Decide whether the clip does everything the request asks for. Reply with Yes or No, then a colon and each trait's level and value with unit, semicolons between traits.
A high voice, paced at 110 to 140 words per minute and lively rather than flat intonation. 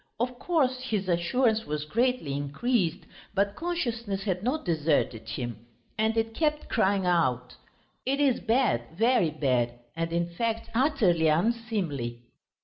Yes: high, 200 Hz; slow, 135 wpm; wide, 7.7 semitones